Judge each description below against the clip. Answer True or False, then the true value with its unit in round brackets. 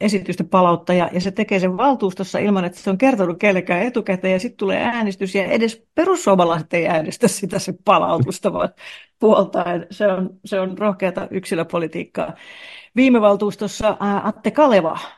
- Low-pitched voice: False (195 Hz)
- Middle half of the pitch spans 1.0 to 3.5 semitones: True (2.4 semitones)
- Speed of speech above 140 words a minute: True (155 wpm)